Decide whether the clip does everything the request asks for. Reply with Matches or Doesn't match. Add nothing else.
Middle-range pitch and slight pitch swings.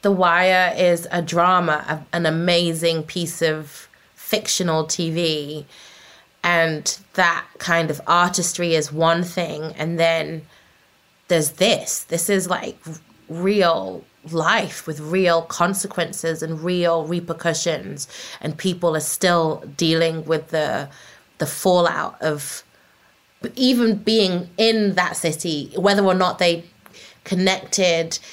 Matches